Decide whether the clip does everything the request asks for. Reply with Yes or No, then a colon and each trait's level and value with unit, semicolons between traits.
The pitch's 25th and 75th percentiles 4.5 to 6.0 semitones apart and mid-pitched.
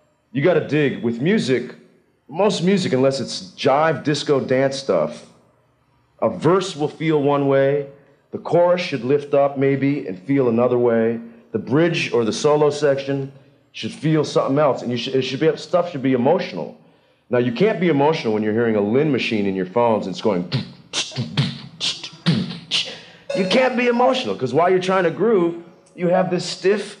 Yes: average, 5.1 semitones; medium, 145 Hz